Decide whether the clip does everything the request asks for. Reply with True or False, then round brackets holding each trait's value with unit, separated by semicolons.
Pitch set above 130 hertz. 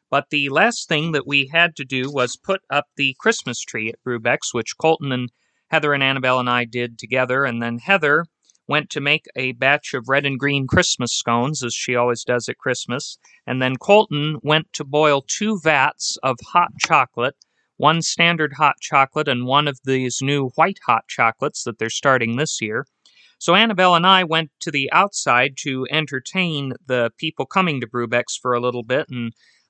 True (140 Hz)